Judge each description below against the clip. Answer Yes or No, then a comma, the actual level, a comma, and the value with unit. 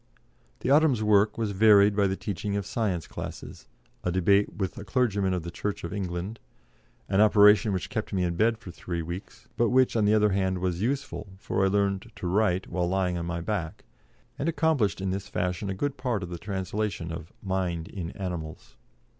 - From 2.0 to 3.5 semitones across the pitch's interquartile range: Yes, average, 2.9 semitones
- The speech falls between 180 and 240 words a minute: Yes, fast, 205 wpm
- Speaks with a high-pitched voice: No, low, 100 Hz